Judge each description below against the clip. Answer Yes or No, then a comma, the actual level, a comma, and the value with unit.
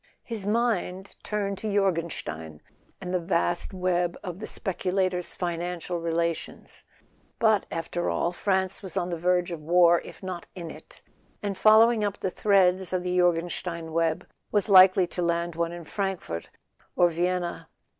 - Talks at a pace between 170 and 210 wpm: No, average, 155 wpm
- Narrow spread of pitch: Yes, narrow, 2.2 semitones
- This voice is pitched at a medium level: Yes, medium, 180 Hz